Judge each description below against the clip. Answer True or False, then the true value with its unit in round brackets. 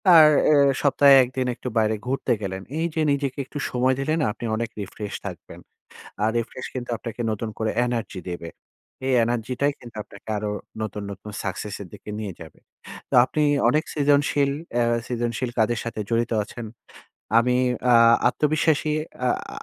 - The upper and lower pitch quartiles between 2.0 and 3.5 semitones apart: False (4.3 semitones)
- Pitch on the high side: False (120 Hz)